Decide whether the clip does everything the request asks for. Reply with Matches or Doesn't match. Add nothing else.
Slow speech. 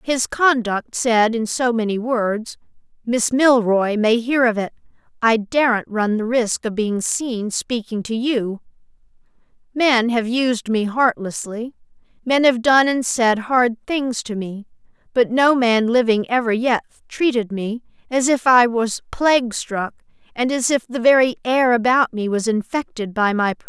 Doesn't match